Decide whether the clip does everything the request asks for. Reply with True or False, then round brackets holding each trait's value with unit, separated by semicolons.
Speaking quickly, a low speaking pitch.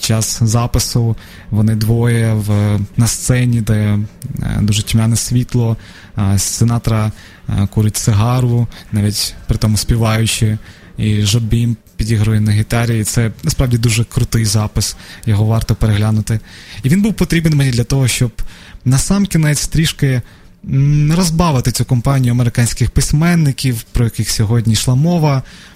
False (135 wpm; 115 Hz)